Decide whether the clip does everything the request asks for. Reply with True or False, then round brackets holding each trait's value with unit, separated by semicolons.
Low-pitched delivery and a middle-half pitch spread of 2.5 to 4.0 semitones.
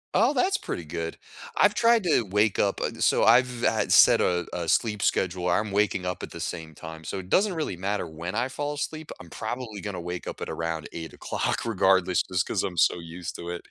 False (95 Hz; 5.3 semitones)